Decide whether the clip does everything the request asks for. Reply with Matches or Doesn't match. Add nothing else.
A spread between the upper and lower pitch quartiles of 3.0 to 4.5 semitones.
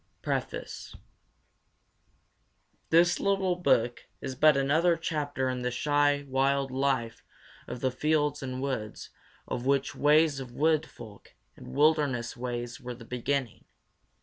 Matches